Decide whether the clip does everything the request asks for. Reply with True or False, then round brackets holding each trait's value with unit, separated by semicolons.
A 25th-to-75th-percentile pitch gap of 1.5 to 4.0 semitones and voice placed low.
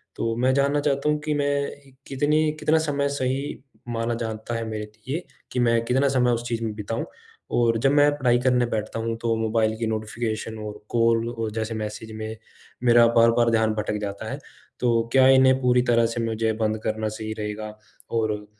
True (2.9 semitones; 115 Hz)